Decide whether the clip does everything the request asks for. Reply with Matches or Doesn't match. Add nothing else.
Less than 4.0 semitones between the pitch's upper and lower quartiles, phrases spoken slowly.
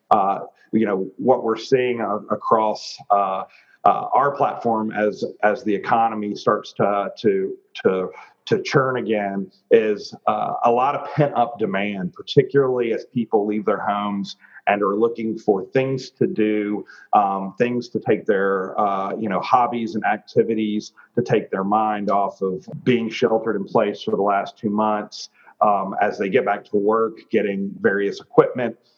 Doesn't match